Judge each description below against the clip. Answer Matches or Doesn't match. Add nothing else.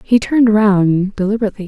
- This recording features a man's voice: Doesn't match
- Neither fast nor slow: Matches